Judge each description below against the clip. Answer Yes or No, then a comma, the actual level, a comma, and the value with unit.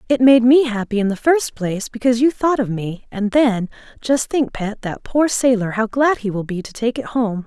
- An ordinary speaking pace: No, fast, 240 wpm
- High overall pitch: Yes, high, 230 Hz